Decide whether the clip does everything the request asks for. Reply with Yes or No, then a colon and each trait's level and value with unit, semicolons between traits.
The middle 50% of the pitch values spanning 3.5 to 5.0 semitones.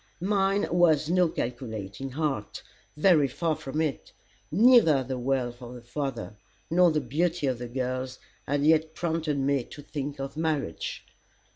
Yes: average, 4.0 semitones